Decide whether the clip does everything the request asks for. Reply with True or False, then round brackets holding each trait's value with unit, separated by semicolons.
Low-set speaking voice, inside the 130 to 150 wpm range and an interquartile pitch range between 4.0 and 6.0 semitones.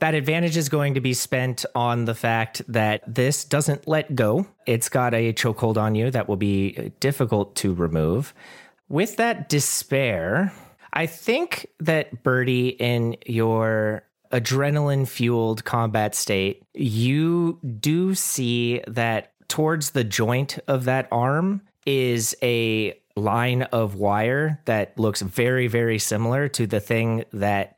True (125 Hz; 140 wpm; 4.4 semitones)